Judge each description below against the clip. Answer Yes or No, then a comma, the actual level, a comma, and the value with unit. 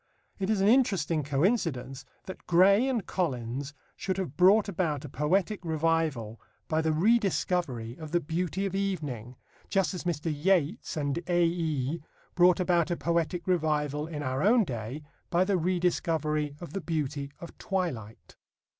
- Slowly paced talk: No, average, 150 wpm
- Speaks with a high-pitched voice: No, medium, 165 Hz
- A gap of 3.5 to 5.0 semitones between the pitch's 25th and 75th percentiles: Yes, average, 4.0 semitones